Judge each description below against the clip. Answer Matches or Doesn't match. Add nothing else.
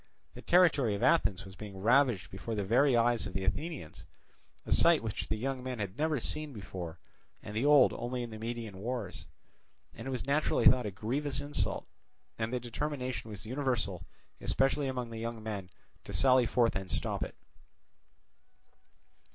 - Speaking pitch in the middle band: Doesn't match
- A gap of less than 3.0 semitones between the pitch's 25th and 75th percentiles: Doesn't match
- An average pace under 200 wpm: Matches